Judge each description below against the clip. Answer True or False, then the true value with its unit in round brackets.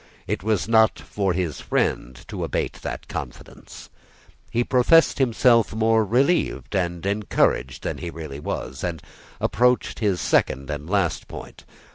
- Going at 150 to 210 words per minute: False (140 wpm)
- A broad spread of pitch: True (5.7 semitones)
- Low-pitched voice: True (100 Hz)